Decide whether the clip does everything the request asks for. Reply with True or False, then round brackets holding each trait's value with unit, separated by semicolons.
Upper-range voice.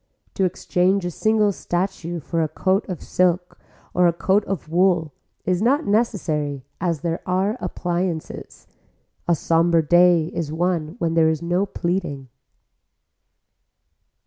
False (175 Hz)